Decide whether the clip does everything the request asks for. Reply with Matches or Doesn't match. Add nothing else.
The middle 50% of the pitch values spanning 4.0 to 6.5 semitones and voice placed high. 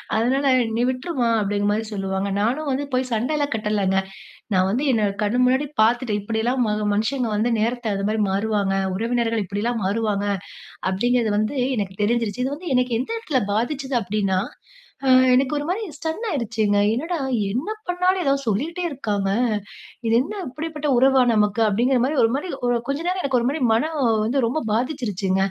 Matches